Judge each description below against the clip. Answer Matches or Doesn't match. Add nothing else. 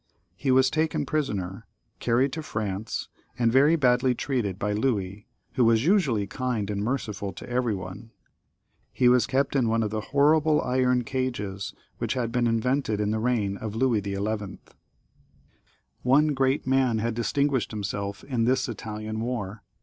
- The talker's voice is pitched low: Matches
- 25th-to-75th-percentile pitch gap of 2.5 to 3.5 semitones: Doesn't match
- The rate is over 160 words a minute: Doesn't match